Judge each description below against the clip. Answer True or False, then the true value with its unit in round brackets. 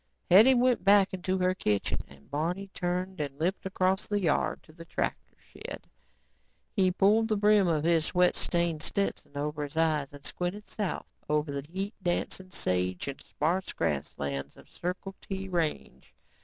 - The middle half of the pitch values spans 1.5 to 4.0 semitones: False (4.4 semitones)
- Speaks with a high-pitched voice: False (175 Hz)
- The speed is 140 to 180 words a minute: True (165 wpm)